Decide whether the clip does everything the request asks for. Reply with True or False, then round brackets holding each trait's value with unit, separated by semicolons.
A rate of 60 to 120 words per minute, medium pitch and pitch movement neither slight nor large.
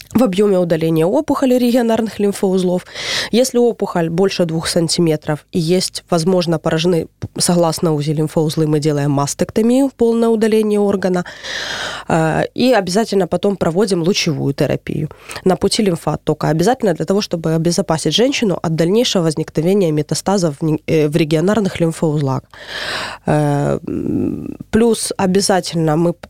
True (110 wpm; 175 Hz; 4.1 semitones)